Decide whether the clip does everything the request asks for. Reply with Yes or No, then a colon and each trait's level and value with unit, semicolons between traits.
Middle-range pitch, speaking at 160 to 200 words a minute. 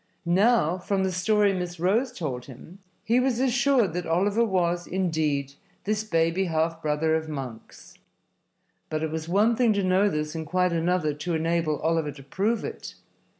Yes: medium, 175 Hz; average, 170 wpm